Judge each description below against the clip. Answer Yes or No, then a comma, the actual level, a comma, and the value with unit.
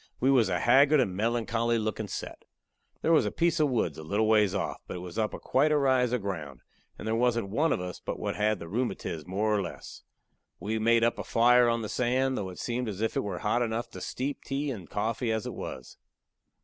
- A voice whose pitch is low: Yes, low, 115 Hz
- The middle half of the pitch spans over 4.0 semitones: No, average, 3.6 semitones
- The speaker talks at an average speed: No, fast, 240 wpm